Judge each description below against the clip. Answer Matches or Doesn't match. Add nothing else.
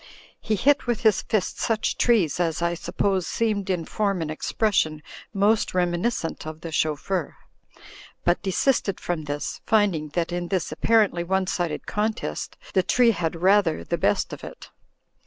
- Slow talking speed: Doesn't match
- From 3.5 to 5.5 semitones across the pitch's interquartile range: Matches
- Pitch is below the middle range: Doesn't match